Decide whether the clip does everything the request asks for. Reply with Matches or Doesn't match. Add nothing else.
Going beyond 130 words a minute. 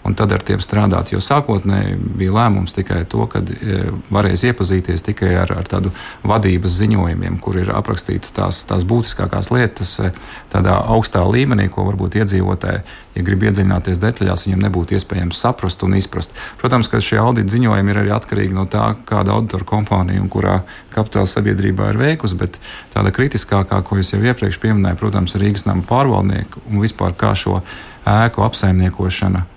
Matches